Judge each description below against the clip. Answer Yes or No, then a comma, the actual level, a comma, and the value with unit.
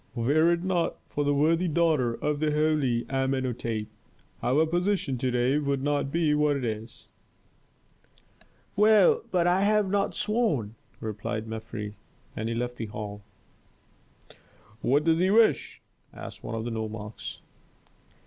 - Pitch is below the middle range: No, medium, 145 Hz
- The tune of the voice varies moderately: No, wide, 6.4 semitones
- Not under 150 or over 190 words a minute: No, average, 140 wpm